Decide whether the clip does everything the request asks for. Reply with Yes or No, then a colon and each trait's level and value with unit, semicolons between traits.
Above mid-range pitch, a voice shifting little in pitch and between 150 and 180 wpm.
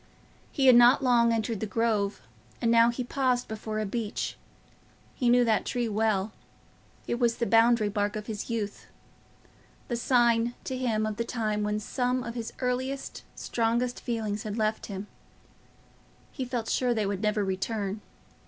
Yes: high, 230 Hz; narrow, 2.3 semitones; average, 160 wpm